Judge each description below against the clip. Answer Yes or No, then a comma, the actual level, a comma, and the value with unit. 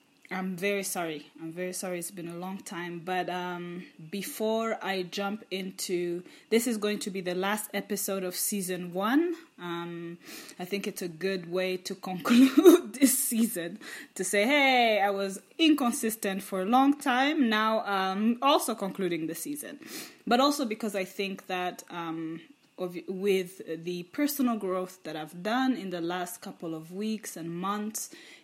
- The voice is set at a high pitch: Yes, high, 195 Hz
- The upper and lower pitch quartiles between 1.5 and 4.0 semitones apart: No, average, 4.4 semitones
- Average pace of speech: Yes, average, 165 wpm